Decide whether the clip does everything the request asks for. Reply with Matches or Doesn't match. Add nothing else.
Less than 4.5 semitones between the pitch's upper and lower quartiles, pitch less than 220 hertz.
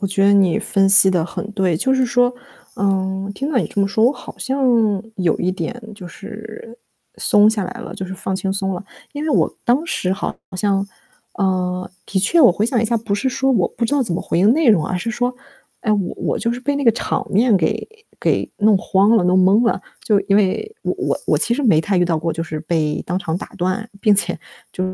Matches